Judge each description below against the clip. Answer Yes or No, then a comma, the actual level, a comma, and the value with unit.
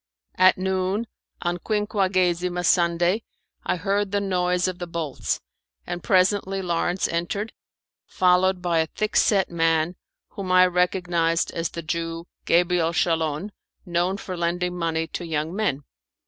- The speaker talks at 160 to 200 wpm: No, slow, 135 wpm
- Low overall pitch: No, medium, 180 Hz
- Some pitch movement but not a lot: No, narrow, 2.0 semitones